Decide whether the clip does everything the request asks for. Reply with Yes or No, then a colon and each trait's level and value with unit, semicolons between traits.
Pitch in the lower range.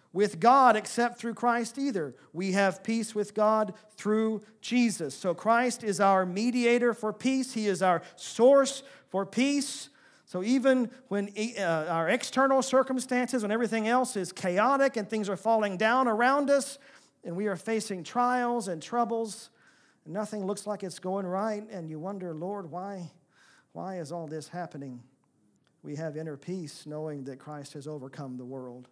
No: high, 210 Hz